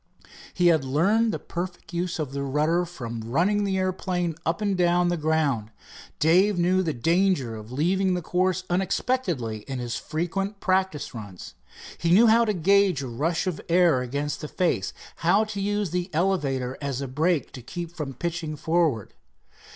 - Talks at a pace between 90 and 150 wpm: No, average, 175 wpm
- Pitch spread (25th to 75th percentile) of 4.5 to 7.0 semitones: Yes, average, 4.9 semitones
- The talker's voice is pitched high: No, medium, 170 Hz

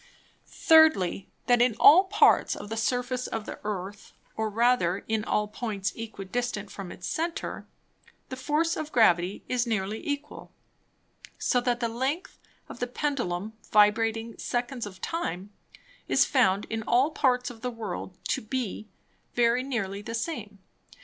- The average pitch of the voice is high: Yes, high, 230 Hz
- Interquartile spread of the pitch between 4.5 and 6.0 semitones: No, average, 3.5 semitones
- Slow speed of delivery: No, average, 150 wpm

